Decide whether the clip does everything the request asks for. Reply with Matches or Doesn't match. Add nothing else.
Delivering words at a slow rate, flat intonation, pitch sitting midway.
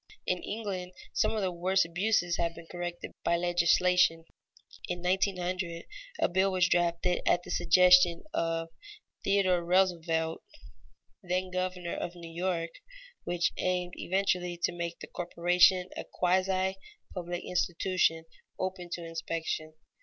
Matches